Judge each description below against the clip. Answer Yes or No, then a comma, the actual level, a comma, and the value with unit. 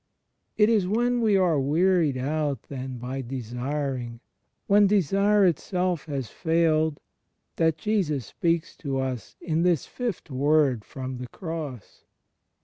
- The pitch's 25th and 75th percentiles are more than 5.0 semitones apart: Yes, wide, 5.6 semitones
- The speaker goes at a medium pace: No, slow, 130 wpm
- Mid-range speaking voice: Yes, medium, 155 Hz